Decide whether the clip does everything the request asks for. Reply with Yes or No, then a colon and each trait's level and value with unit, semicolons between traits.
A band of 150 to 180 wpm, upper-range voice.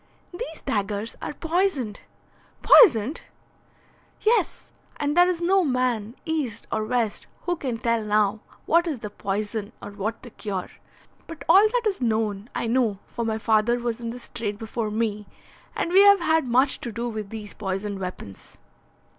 Yes: average, 165 wpm; high, 230 Hz